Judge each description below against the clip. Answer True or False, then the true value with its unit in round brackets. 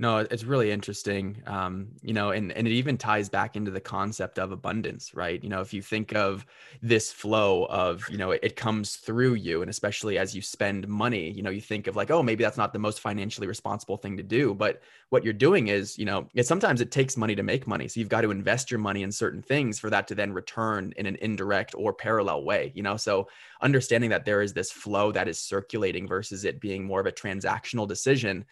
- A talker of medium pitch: False (105 Hz)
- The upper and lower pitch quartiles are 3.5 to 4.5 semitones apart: False (2.7 semitones)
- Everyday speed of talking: False (240 wpm)